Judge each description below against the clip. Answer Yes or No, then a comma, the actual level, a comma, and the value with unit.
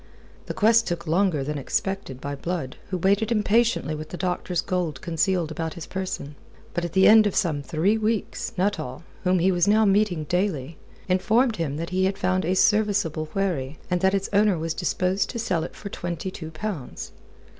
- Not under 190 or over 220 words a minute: Yes, average, 195 wpm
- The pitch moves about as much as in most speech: Yes, average, 3.8 semitones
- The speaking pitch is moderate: Yes, medium, 180 Hz